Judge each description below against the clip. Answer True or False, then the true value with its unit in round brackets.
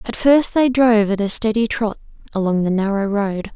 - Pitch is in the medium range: False (215 Hz)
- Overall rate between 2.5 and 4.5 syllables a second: False (5.2 syllables/s)